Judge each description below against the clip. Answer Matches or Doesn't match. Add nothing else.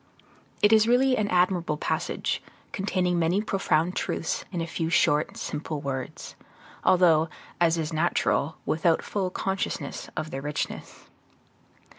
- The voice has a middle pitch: Matches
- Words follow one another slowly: Matches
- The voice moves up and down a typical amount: Matches